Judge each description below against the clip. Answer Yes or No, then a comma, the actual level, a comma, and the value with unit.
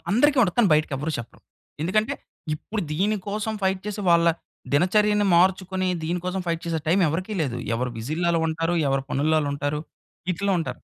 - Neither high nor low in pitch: Yes, medium, 175 Hz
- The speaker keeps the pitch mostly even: No, average, 4.5 semitones